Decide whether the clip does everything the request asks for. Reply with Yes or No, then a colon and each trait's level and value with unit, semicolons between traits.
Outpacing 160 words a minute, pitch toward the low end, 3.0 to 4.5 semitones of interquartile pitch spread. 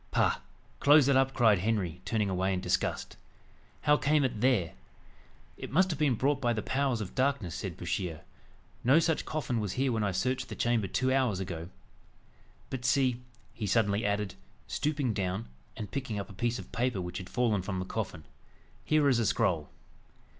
No: average, 185 wpm; low, 115 Hz; wide, 5.4 semitones